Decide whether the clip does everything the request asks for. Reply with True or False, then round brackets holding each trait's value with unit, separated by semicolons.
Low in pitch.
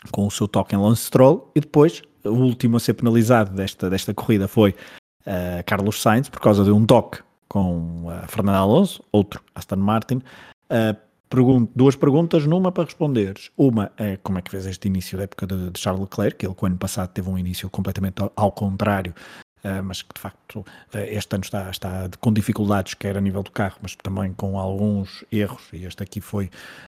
True (100 Hz)